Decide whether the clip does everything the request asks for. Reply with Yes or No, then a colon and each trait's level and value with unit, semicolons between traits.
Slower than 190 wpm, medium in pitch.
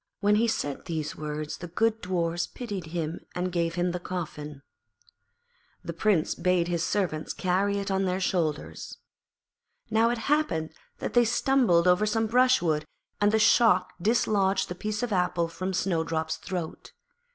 Yes: average, 160 wpm; medium, 180 Hz